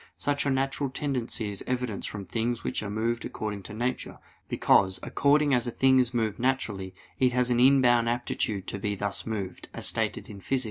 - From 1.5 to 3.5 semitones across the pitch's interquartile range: No, average, 3.9 semitones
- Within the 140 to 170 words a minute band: No, average, 195 wpm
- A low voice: Yes, low, 120 Hz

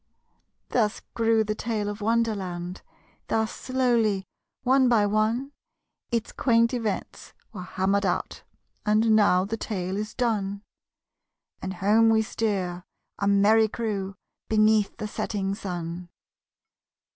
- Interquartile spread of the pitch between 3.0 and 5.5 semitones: No, narrow, 2.5 semitones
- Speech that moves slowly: Yes, slow, 120 wpm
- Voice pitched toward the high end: Yes, high, 215 Hz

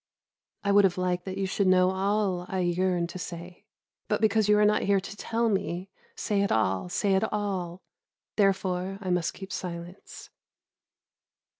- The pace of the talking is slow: No, average, 165 wpm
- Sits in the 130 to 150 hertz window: No, high, 190 Hz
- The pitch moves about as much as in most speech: No, narrow, 2.0 semitones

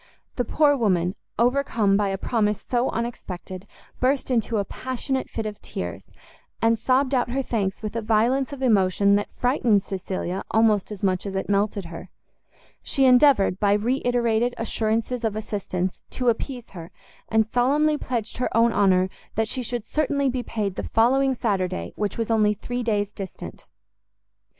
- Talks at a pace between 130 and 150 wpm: No, average, 165 wpm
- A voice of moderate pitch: No, high, 225 Hz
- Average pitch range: Yes, average, 3.7 semitones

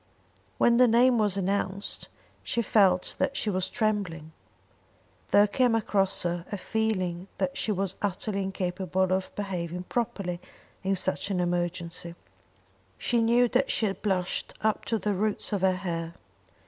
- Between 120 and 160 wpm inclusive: Yes, average, 150 wpm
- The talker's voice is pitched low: No, high, 195 Hz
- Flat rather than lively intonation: No, average, 3.1 semitones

